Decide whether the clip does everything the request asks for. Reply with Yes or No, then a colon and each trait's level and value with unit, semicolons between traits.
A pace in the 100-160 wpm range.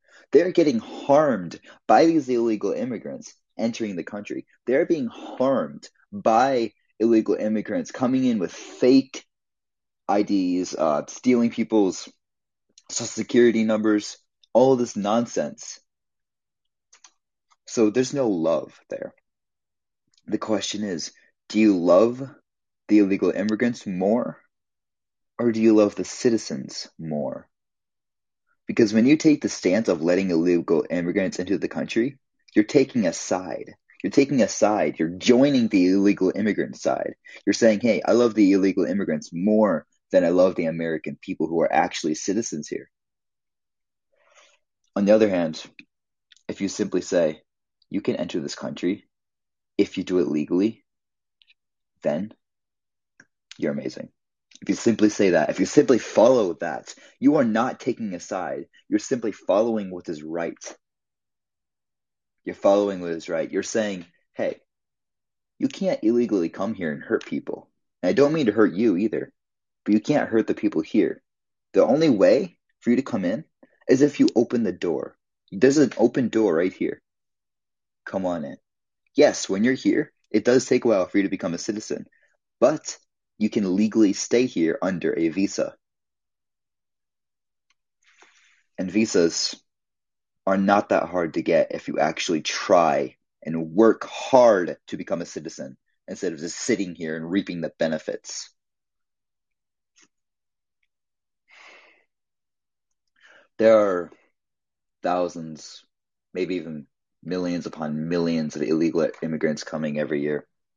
Yes: average, 140 wpm